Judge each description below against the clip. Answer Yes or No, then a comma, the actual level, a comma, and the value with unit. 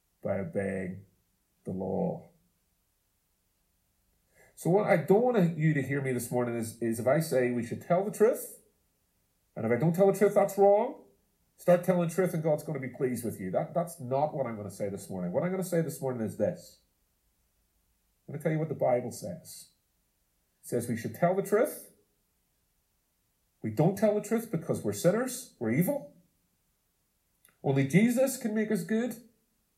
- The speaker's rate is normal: Yes, average, 195 wpm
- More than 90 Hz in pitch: Yes, medium, 140 Hz